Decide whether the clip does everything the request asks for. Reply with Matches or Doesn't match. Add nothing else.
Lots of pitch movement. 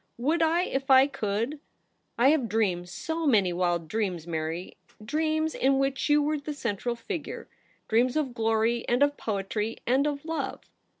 Matches